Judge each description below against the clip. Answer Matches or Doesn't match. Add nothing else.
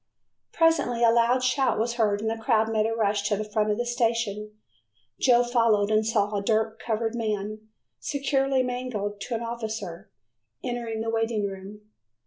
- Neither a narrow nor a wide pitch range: Doesn't match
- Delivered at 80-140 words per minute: Doesn't match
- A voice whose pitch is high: Matches